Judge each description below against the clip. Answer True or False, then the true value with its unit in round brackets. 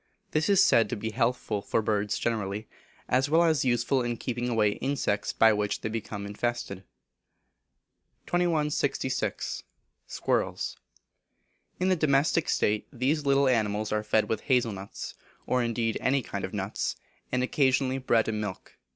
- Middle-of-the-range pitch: False (120 Hz)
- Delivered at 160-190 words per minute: False (150 wpm)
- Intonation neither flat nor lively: True (4.3 semitones)